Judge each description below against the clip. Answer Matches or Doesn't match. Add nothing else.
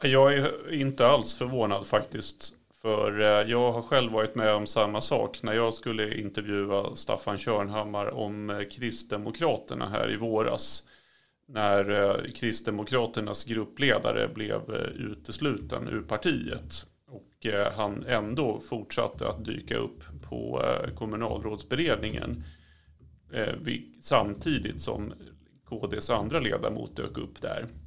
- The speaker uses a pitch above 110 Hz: Doesn't match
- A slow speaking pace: Matches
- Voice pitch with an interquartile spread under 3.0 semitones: Matches